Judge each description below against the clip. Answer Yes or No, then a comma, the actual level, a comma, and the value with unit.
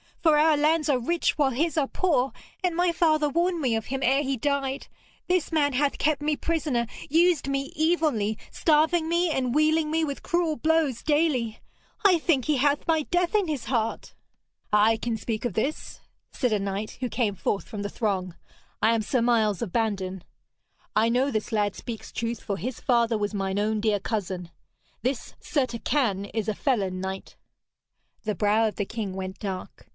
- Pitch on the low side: No, very high, 255 Hz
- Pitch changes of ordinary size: No, wide, 6.2 semitones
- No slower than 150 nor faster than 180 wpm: No, average, 190 wpm